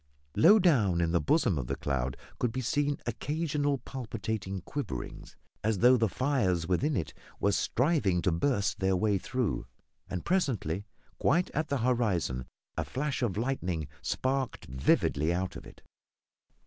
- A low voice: Yes, low, 110 Hz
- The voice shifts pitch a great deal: Yes, wide, 7.6 semitones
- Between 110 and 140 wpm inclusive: No, average, 150 wpm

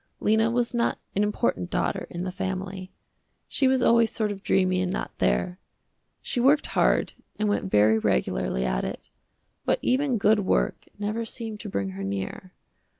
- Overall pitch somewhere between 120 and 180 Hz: No, high, 205 Hz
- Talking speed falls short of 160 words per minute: No, average, 170 wpm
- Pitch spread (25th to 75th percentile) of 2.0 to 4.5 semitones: Yes, average, 4.0 semitones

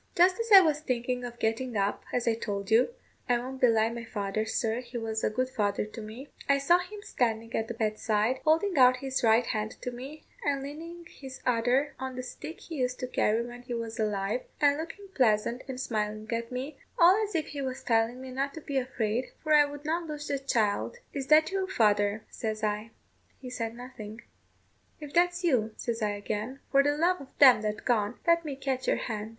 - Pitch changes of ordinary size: Yes, average, 4.4 semitones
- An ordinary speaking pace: No, fast, 215 wpm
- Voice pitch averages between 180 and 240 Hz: No, very high, 250 Hz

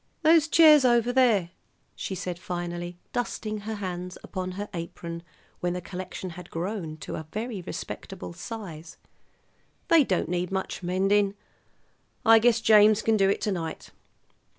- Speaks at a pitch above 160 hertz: Yes, high, 190 Hz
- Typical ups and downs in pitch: Yes, average, 3.9 semitones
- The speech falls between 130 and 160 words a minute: Yes, average, 150 wpm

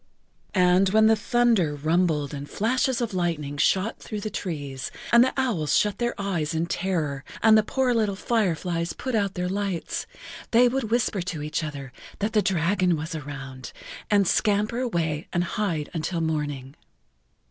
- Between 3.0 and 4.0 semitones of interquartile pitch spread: No, wide, 5.6 semitones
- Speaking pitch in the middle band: Yes, medium, 180 Hz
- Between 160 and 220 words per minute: Yes, average, 165 wpm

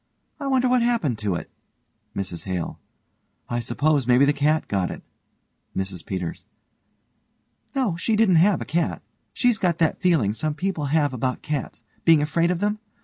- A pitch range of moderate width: No, wide, 7.7 semitones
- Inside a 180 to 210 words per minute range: No, average, 165 wpm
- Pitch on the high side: No, medium, 155 Hz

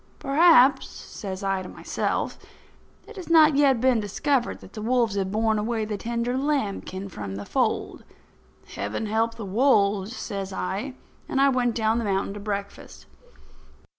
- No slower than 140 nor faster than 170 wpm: Yes, average, 160 wpm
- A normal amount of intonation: Yes, average, 4.5 semitones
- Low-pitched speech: No, high, 220 Hz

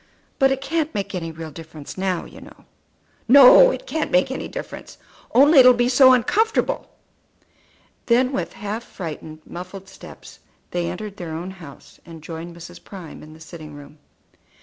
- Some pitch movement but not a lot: No, wide, 7.7 semitones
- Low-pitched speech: No, high, 190 Hz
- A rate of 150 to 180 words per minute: Yes, average, 170 wpm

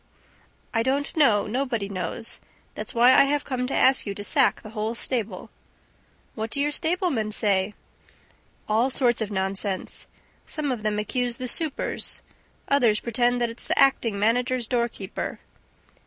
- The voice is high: Yes, high, 235 Hz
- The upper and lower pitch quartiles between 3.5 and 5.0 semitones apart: Yes, average, 3.8 semitones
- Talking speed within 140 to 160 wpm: Yes, average, 155 wpm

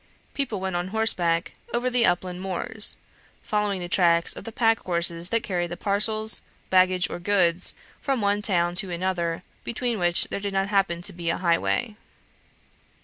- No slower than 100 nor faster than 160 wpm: No, average, 170 wpm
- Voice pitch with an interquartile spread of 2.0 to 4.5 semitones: Yes, average, 3.4 semitones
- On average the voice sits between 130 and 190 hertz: Yes, medium, 185 Hz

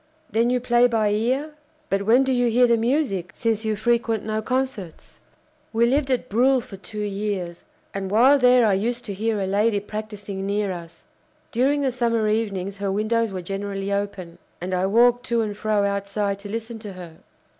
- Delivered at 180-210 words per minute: Yes, average, 190 wpm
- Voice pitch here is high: Yes, high, 215 Hz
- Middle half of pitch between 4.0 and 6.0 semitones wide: No, average, 3.2 semitones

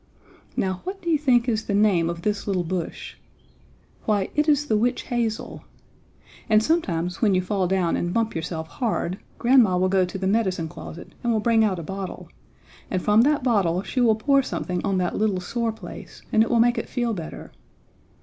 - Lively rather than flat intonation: No, average, 4.5 semitones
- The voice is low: No, high, 210 Hz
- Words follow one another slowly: No, average, 200 wpm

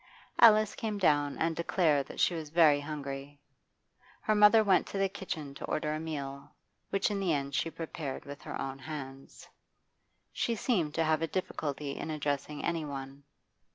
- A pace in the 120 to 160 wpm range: No, average, 175 wpm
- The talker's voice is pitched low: No, medium, 155 Hz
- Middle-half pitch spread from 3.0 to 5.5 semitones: Yes, average, 4.3 semitones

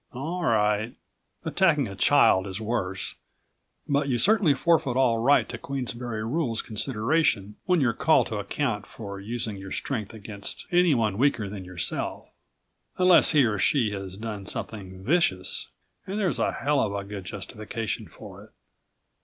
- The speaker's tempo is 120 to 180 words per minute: Yes, average, 155 wpm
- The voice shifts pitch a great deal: Yes, wide, 5.8 semitones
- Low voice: Yes, low, 115 Hz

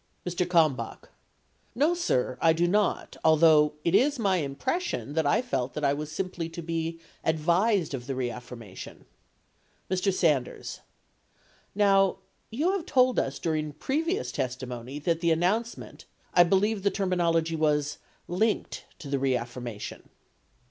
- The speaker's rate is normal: Yes, average, 150 wpm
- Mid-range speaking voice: Yes, medium, 165 Hz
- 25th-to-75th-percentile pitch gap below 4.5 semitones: No, wide, 5.5 semitones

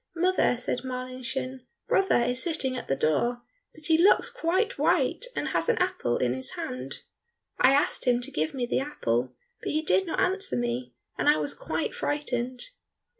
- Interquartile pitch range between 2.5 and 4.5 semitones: No, wide, 5.6 semitones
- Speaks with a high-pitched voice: Yes, very high, 255 Hz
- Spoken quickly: No, average, 180 wpm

